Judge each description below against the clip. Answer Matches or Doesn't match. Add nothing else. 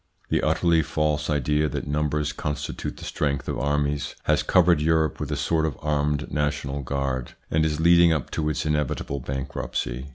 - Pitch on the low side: Matches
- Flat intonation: Matches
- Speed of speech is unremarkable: Matches